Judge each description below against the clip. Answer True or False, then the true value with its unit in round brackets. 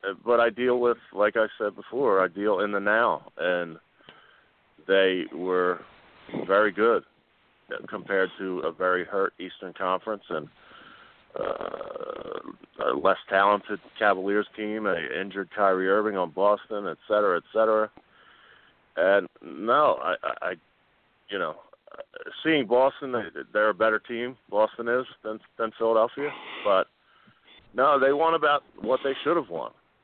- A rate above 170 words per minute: False (140 wpm)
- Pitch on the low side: True (110 Hz)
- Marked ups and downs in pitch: False (4.0 semitones)